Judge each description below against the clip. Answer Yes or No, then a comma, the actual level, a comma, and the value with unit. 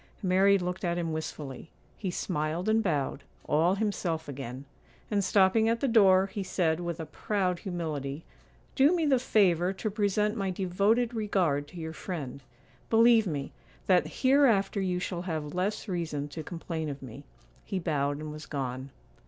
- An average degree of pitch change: Yes, average, 4.6 semitones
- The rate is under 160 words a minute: No, average, 165 wpm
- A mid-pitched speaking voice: Yes, medium, 180 Hz